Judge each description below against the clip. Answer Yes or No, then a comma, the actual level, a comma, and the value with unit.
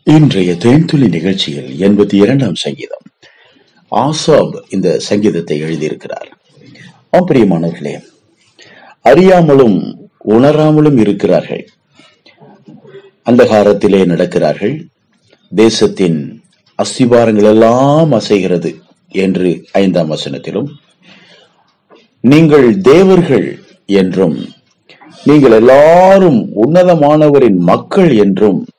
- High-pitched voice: No, low, 110 Hz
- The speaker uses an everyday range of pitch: No, wide, 8.2 semitones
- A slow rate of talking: Yes, slow, 60 wpm